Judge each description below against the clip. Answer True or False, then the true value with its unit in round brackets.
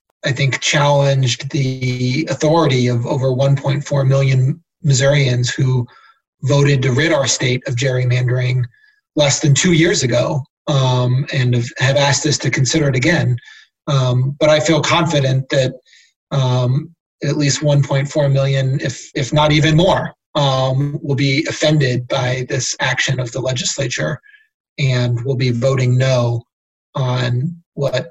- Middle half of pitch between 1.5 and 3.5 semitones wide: True (2.6 semitones)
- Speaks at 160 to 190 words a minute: False (140 wpm)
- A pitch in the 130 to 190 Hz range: True (135 Hz)